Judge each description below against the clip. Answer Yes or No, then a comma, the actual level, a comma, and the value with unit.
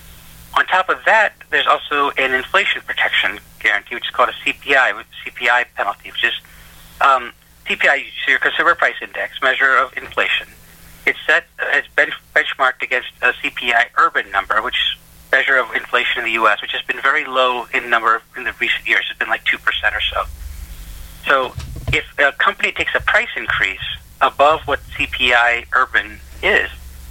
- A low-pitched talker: Yes, low, 120 Hz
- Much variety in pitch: Yes, wide, 9.0 semitones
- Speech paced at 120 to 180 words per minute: Yes, average, 170 wpm